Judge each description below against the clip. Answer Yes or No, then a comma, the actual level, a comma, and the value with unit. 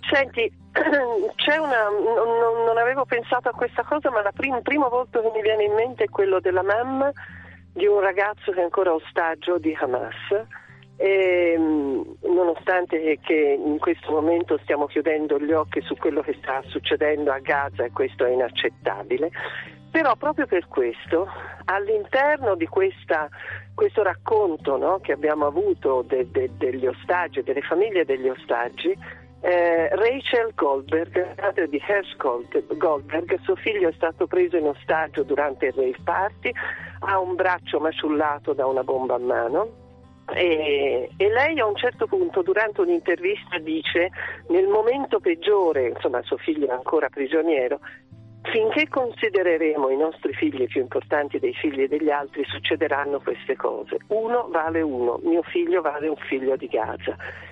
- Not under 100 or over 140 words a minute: No, average, 150 wpm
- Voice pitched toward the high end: Yes, high, 210 Hz